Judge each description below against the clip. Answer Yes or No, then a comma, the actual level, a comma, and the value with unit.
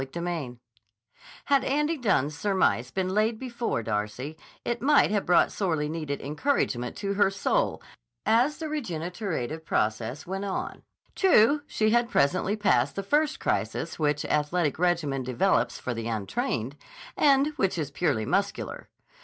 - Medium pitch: Yes, medium, 180 Hz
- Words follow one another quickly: No, average, 145 wpm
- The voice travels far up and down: Yes, wide, 7.7 semitones